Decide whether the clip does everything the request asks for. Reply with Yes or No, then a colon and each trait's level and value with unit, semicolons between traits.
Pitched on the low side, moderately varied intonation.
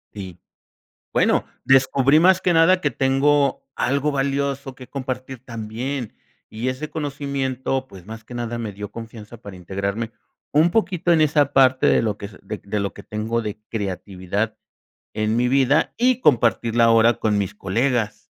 Yes: low, 125 Hz; average, 4.5 semitones